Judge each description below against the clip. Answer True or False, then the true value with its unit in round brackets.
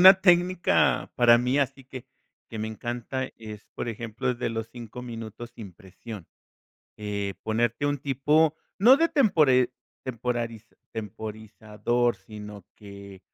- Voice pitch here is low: True (120 Hz)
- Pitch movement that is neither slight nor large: True (3.5 semitones)